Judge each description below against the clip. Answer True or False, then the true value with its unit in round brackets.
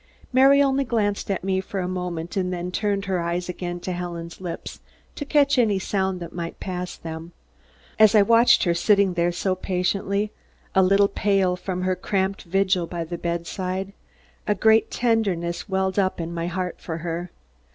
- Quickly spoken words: False (185 wpm)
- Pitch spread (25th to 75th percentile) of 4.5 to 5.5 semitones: False (2.4 semitones)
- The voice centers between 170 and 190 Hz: True (185 Hz)